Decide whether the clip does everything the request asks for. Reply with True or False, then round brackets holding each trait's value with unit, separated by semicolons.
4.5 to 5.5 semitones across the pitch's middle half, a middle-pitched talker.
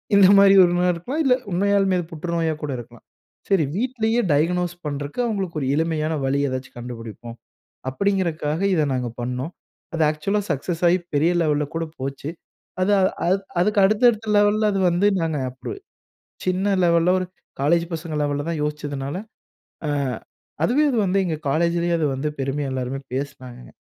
True (5.1 semitones; 165 Hz)